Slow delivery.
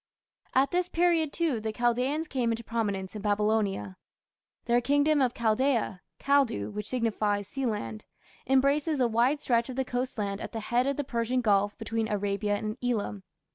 No: average, 170 wpm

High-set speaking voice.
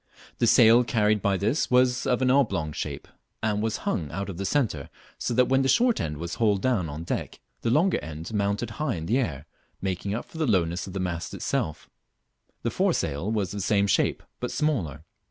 No: low, 105 Hz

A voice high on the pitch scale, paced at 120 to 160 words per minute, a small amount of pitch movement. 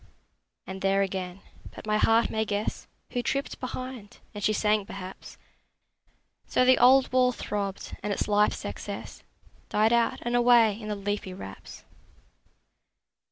No: high, 215 Hz; average, 145 wpm; average, 3.3 semitones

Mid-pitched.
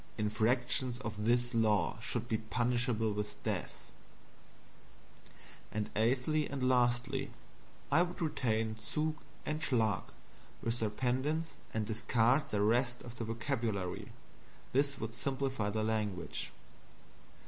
No: low, 120 Hz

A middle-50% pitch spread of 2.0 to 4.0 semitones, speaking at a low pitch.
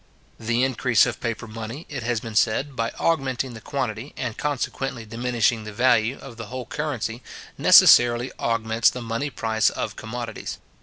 Yes: narrow, 2.4 semitones; low, 120 Hz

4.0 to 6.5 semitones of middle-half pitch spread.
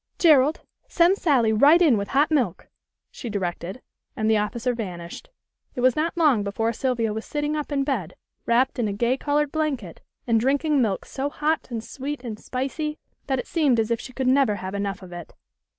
Yes: average, 5.2 semitones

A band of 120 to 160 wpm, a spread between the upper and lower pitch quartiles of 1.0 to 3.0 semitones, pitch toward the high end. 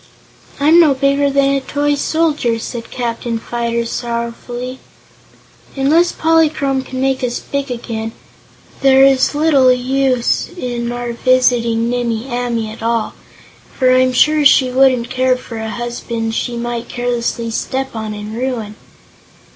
Yes: average, 140 wpm; narrow, 2.5 semitones; very high, 250 Hz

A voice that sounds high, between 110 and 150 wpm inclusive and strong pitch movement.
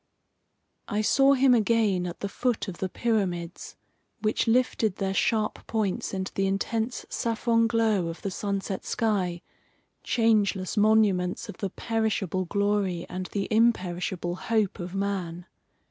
No: high, 200 Hz; slow, 135 wpm; average, 3.2 semitones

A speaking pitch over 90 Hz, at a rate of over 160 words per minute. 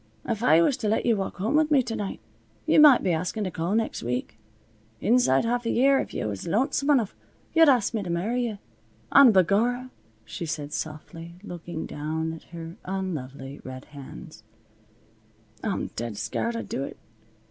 Yes: high, 190 Hz; average, 180 wpm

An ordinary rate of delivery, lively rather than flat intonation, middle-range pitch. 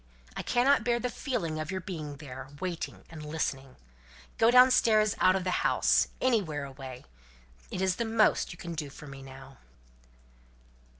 Yes: average, 165 wpm; wide, 7.8 semitones; medium, 170 Hz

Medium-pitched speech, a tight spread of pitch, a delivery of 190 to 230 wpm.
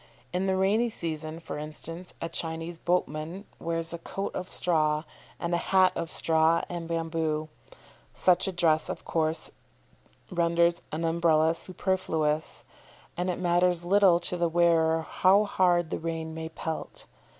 No: medium, 170 Hz; narrow, 1.8 semitones; average, 150 wpm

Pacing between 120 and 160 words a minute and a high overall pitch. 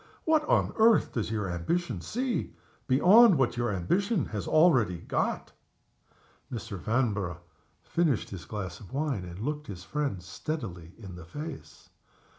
No: average, 140 wpm; low, 120 Hz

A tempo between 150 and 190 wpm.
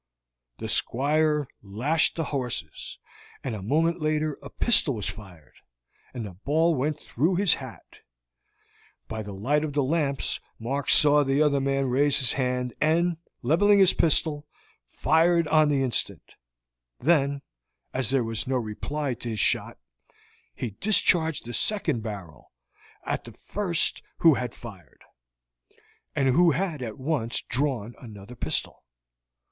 No: average, 140 wpm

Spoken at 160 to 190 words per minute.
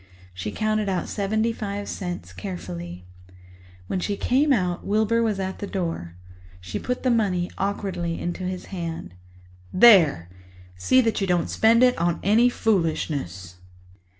No: average, 145 wpm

